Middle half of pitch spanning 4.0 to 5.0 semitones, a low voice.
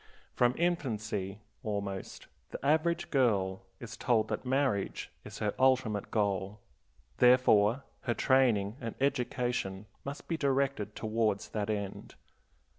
Yes: average, 4.3 semitones; low, 115 Hz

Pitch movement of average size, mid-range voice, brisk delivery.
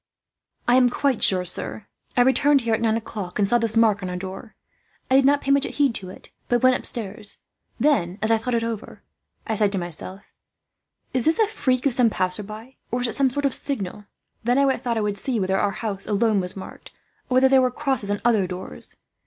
No: average, 4.4 semitones; high, 225 Hz; fast, 225 wpm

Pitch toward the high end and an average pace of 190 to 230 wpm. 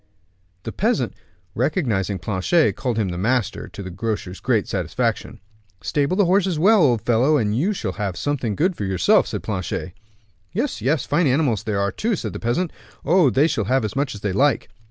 No: low, 125 Hz; average, 195 wpm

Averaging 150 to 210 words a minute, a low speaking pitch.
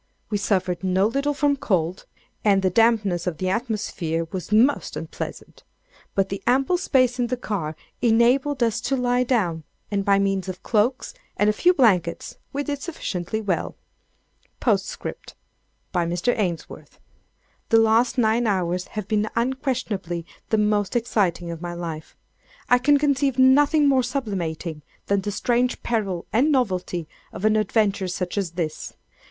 No: average, 155 wpm; high, 210 Hz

